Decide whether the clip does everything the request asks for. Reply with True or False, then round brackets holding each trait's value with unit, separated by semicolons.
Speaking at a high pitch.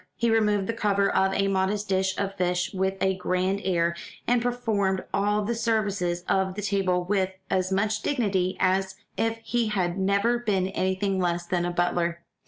True (195 Hz)